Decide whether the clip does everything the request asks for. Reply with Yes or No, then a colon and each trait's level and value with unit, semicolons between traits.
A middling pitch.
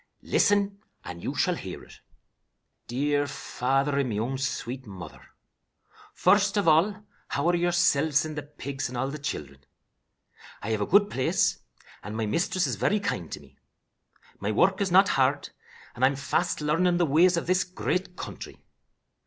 Yes: medium, 145 Hz